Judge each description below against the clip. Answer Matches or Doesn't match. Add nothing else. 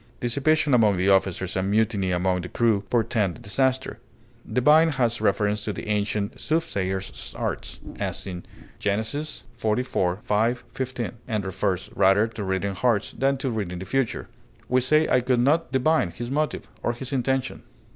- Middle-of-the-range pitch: Doesn't match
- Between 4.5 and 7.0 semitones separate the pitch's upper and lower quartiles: Matches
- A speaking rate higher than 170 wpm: Doesn't match